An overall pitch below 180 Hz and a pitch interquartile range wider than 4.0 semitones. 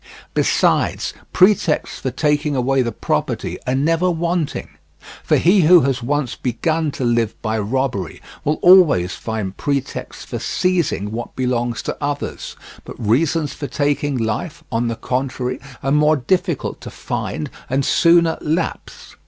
Yes: medium, 140 Hz; average, 5.1 semitones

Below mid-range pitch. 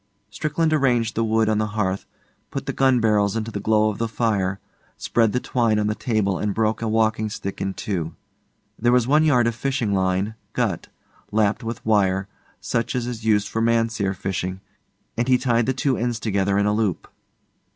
Yes: low, 110 Hz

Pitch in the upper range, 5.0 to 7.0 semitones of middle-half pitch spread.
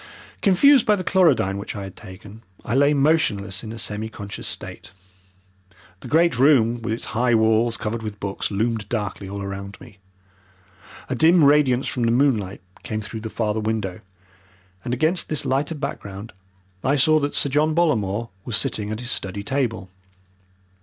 No: low, 115 Hz; wide, 5.5 semitones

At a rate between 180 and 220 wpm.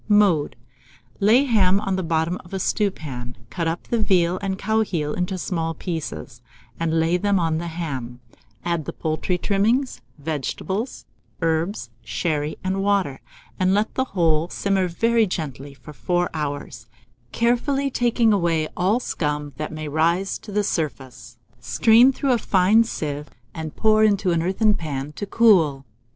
No: average, 160 wpm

